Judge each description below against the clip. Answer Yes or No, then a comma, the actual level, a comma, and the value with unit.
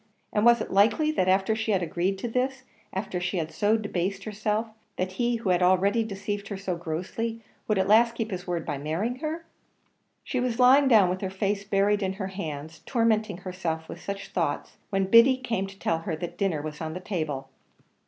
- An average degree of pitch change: Yes, average, 3.8 semitones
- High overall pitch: Yes, high, 195 Hz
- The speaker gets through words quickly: Yes, fast, 210 wpm